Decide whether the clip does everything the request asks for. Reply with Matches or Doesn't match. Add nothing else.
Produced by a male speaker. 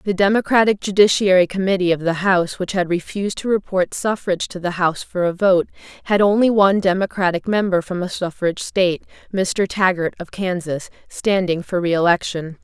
Doesn't match